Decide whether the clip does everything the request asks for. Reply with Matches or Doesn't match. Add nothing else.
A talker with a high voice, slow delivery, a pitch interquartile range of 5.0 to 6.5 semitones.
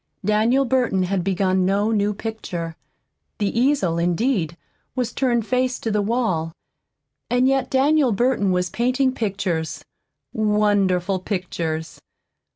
Matches